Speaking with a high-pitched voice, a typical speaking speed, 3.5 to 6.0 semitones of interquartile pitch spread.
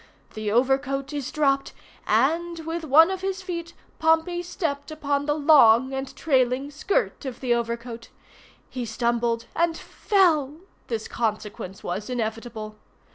No: very high, 275 Hz; slow, 130 wpm; wide, 5.5 semitones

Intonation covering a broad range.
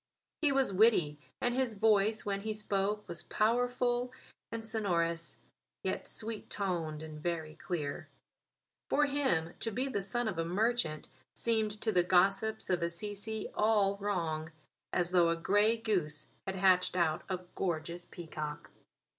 No: average, 4.5 semitones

